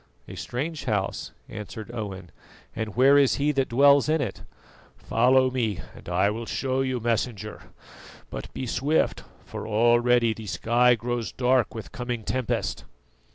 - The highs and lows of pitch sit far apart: No, average, 2.8 semitones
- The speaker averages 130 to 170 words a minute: Yes, average, 150 wpm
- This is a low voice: Yes, low, 120 Hz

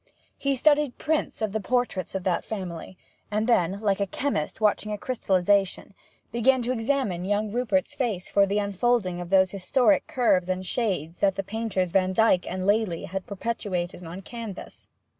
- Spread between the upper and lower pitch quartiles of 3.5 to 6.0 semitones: Yes, average, 4.2 semitones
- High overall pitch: Yes, high, 200 Hz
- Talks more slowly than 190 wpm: Yes, average, 165 wpm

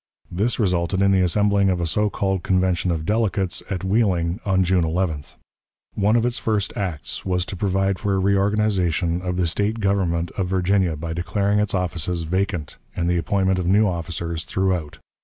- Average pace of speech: Yes, average, 180 wpm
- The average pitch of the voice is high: No, very low, 95 Hz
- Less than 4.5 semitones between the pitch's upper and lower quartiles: Yes, narrow, 2.5 semitones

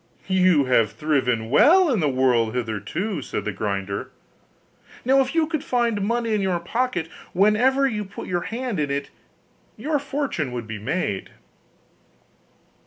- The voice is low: No, medium, 185 Hz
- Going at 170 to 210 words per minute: No, average, 150 wpm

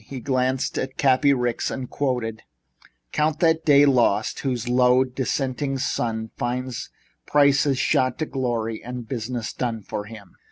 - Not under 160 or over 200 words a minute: No, average, 145 wpm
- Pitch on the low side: Yes, low, 125 Hz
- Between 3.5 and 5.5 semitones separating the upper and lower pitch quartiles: No, narrow, 2.4 semitones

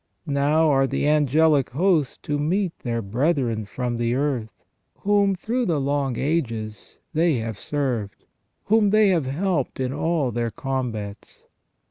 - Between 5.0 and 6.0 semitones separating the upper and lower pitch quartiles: Yes, wide, 5.5 semitones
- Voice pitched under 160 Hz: Yes, medium, 140 Hz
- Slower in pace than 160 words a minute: Yes, average, 140 wpm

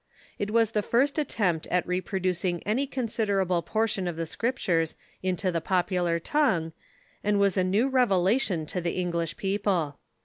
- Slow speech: No, average, 160 wpm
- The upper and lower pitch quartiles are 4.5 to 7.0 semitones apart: No, average, 4.0 semitones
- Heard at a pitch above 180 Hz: Yes, high, 190 Hz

